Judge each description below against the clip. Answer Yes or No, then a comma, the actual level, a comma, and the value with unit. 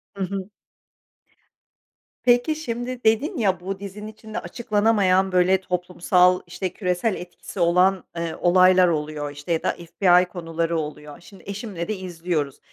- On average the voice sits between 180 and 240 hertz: Yes, medium, 185 Hz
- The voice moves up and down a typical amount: Yes, average, 3.1 semitones